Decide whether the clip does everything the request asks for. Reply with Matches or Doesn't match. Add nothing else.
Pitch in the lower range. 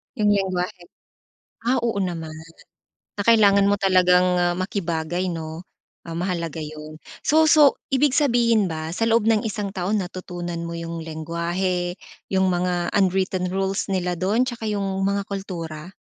Doesn't match